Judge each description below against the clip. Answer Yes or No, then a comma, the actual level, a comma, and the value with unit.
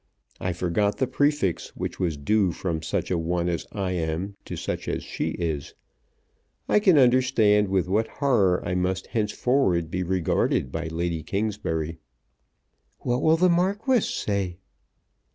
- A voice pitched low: Yes, very low, 95 Hz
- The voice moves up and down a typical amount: No, wide, 6.2 semitones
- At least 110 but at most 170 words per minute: Yes, average, 150 wpm